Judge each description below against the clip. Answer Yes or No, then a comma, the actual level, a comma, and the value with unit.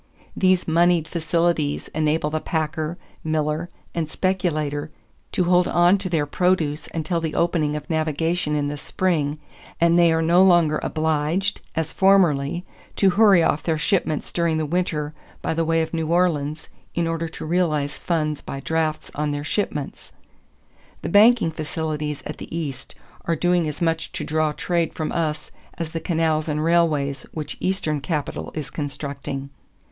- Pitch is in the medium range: Yes, medium, 160 Hz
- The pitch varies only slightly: Yes, narrow, 2.3 semitones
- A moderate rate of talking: Yes, average, 160 wpm